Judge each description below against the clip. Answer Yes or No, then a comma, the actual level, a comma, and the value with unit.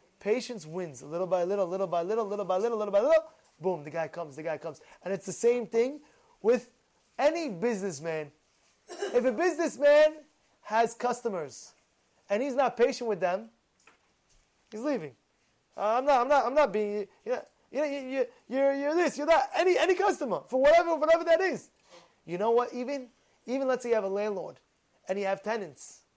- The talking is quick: No, average, 185 wpm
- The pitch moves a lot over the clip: Yes, wide, 7.3 semitones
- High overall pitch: Yes, high, 240 Hz